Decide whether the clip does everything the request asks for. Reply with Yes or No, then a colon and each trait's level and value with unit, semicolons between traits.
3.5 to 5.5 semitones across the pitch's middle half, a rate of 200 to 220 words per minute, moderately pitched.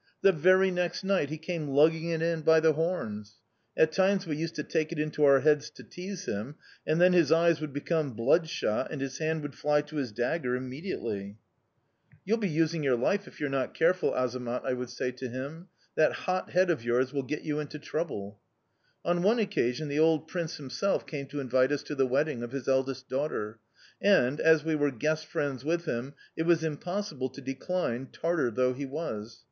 Yes: average, 4.2 semitones; fast, 205 wpm; medium, 150 Hz